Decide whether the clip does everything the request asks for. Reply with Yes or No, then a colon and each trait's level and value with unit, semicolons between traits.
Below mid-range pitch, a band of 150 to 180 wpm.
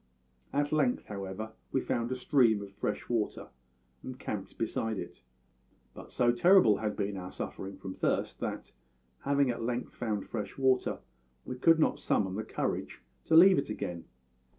Yes: low, 115 Hz; average, 165 wpm